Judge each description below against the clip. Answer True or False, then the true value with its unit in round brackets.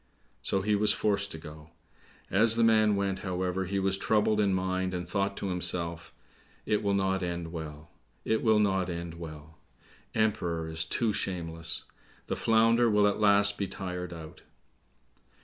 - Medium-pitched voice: False (95 Hz)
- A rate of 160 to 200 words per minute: True (165 wpm)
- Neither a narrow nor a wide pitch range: True (3.4 semitones)